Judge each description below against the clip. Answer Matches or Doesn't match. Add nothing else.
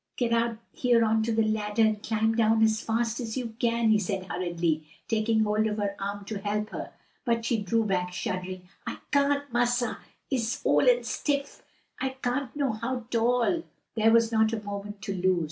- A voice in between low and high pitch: Doesn't match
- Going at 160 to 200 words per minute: Matches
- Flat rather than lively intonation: Matches